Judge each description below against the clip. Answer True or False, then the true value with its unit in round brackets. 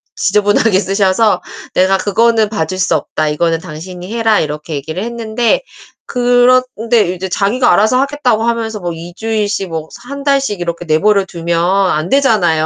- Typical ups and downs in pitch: True (4.8 semitones)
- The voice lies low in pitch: False (200 Hz)